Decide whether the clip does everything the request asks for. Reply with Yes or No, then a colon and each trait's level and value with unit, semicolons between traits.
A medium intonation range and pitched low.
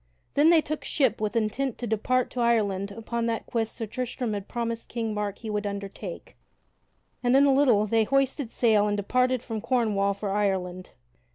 No: average, 3.4 semitones; high, 225 Hz